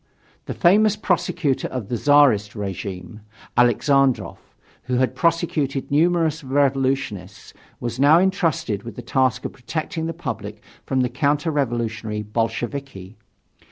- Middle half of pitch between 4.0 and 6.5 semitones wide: Yes, average, 5.2 semitones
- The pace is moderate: No, slow, 125 wpm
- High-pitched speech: No, low, 135 Hz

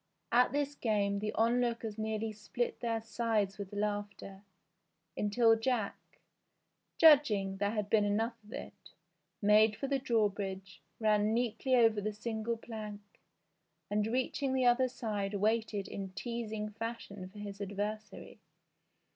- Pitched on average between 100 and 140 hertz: No, high, 215 Hz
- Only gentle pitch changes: Yes, narrow, 2.2 semitones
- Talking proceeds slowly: Yes, slow, 130 wpm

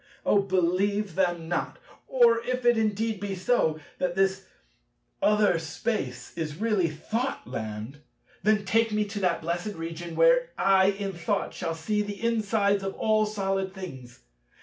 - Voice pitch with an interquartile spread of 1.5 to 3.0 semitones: No, average, 3.8 semitones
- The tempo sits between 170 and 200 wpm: No, average, 150 wpm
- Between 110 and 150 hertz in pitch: No, high, 195 Hz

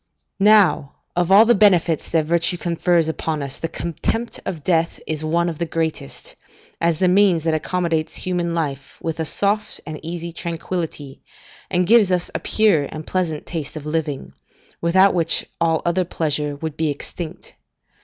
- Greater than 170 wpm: No, average, 165 wpm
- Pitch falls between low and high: Yes, medium, 165 Hz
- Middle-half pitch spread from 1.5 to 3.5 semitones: Yes, narrow, 2.5 semitones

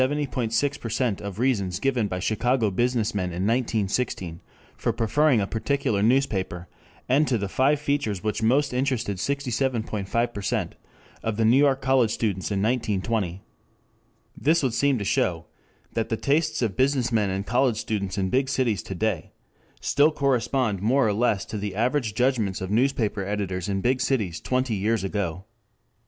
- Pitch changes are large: No, average, 4.6 semitones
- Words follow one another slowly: No, average, 160 wpm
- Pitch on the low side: Yes, low, 115 Hz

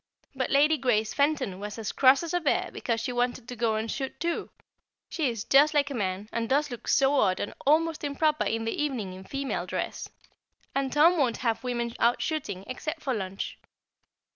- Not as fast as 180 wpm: No, average, 200 wpm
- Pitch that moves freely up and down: No, average, 4.5 semitones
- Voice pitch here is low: No, very high, 255 Hz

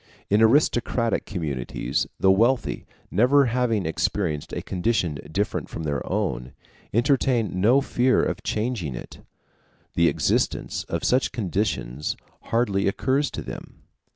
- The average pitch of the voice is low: Yes, low, 105 Hz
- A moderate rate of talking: No, slow, 125 wpm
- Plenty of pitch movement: Yes, wide, 6.2 semitones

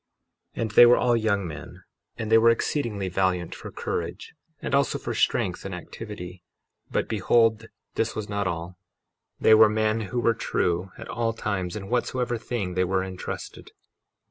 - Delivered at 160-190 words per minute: Yes, average, 170 wpm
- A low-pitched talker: Yes, low, 105 Hz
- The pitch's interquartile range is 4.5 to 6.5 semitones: No, average, 3.7 semitones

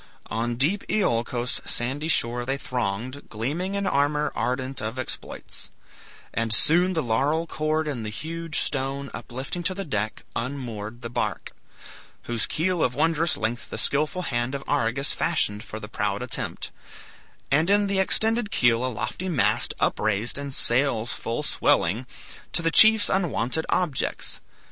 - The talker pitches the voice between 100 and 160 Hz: Yes, low, 135 Hz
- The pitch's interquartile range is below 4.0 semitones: No, wide, 5.6 semitones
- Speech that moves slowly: No, average, 150 wpm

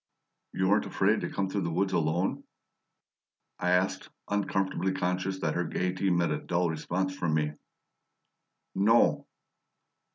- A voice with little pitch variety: Yes, narrow, 2.0 semitones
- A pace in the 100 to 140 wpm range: Yes, slow, 135 wpm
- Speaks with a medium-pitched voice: No, very low, 90 Hz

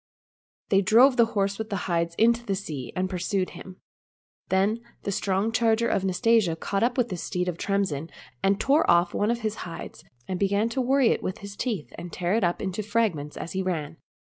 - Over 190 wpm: Yes, average, 200 wpm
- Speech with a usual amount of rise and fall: Yes, average, 3.9 semitones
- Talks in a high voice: Yes, high, 195 Hz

